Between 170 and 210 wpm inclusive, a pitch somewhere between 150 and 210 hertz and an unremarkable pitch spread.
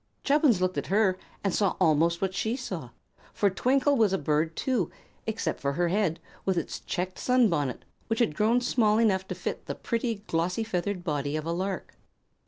Yes: average, 190 wpm; high, 190 Hz; average, 4.8 semitones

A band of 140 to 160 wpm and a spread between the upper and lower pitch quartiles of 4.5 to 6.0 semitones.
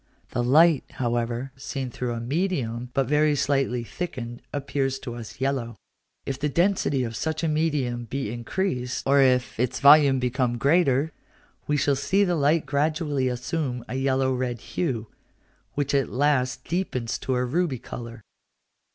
No: average, 155 wpm; average, 3.1 semitones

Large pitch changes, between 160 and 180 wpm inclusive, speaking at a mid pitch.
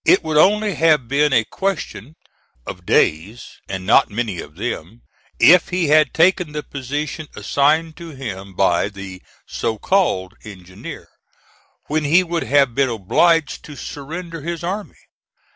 No: wide, 7.3 semitones; average, 145 wpm; medium, 145 Hz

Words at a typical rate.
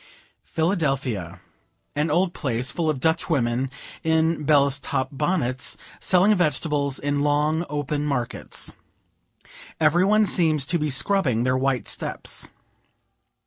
No: slow, 120 wpm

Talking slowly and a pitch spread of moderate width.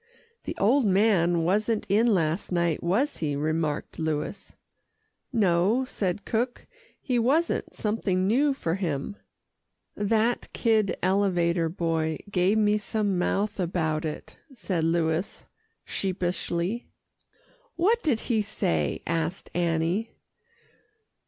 Yes: slow, 110 wpm; average, 4.6 semitones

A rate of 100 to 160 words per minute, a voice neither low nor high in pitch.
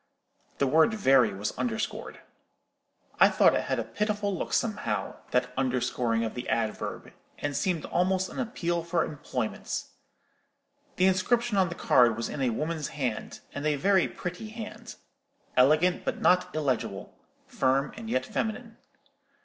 Yes: average, 145 wpm; medium, 155 Hz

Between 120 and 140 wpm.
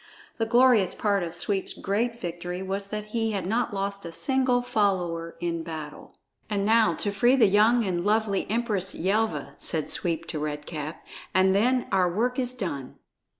No: average, 175 wpm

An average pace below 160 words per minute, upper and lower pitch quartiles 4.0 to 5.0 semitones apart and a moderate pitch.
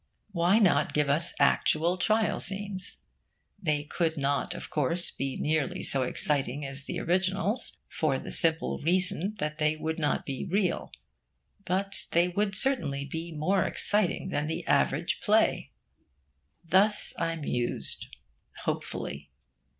Yes: slow, 135 wpm; average, 4.3 semitones; medium, 170 Hz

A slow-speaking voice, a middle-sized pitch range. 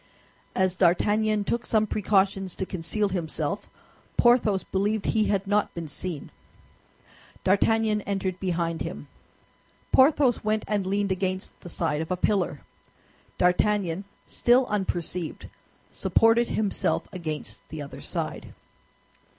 Yes: slow, 120 wpm; average, 3.0 semitones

